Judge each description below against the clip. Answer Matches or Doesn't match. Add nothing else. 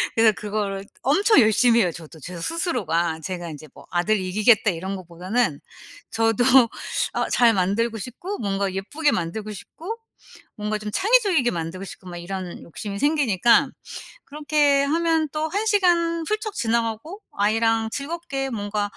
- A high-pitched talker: Matches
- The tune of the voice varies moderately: Doesn't match